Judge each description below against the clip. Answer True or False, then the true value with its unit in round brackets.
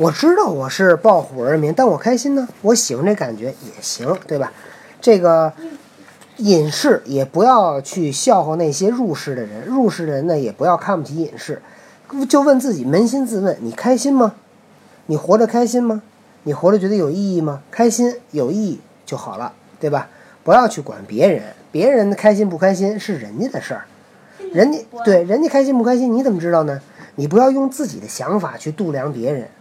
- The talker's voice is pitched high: True (205 Hz)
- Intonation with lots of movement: True (6.9 semitones)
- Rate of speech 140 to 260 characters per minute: False (285 characters per minute)